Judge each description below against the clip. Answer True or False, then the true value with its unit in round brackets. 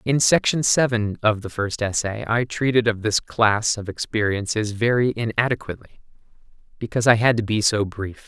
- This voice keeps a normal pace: True (165 wpm)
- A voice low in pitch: True (110 Hz)